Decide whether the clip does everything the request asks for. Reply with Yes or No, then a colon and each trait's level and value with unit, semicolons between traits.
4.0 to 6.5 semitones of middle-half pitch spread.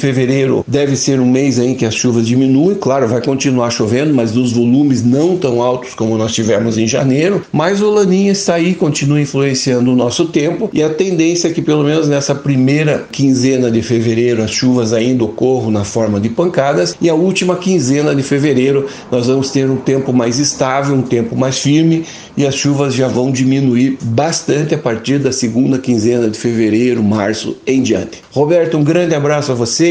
No: average, 3.6 semitones